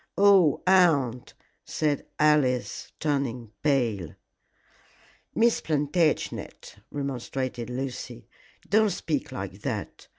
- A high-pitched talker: No, medium, 145 Hz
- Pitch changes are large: No, average, 4.3 semitones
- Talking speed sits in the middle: No, slow, 80 wpm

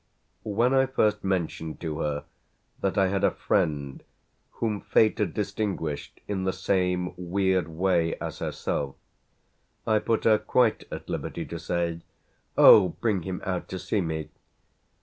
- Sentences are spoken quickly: No, average, 150 wpm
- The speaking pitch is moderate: No, very low, 95 Hz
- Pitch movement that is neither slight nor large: Yes, average, 3.8 semitones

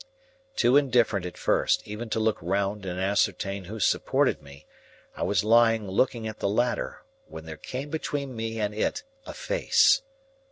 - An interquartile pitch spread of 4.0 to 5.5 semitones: No, average, 3.4 semitones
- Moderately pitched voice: No, low, 110 Hz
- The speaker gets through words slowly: No, average, 165 wpm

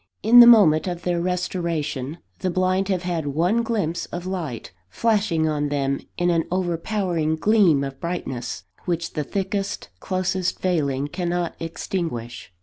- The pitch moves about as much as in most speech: Yes, average, 3.4 semitones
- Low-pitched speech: No, medium, 175 Hz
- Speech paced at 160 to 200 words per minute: No, average, 145 wpm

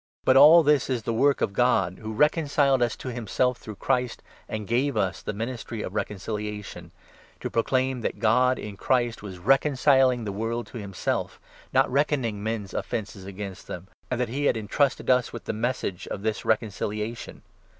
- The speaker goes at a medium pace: Yes, average, 190 wpm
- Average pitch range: Yes, average, 3.6 semitones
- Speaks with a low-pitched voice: Yes, low, 115 Hz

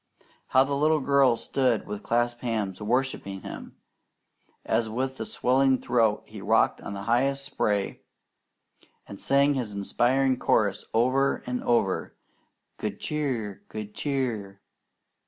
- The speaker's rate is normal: No, slow, 125 wpm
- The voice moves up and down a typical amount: Yes, average, 4.3 semitones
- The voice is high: No, low, 120 Hz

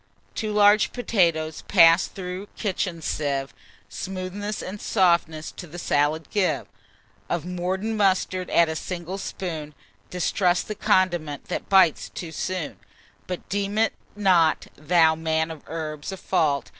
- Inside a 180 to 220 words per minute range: No, slow, 135 wpm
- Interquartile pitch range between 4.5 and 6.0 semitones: No, average, 3.3 semitones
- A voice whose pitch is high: No, medium, 180 Hz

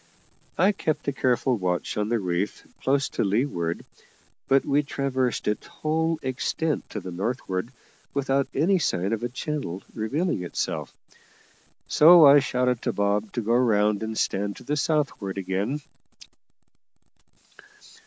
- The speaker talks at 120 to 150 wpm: Yes, average, 140 wpm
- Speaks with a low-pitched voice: Yes, low, 125 Hz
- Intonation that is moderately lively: No, wide, 5.7 semitones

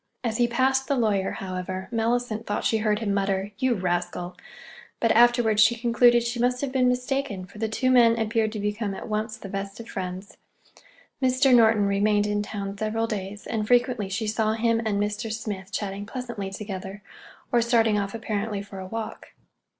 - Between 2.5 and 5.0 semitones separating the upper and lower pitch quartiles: Yes, average, 2.8 semitones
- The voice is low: No, high, 215 Hz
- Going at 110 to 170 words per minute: No, average, 185 wpm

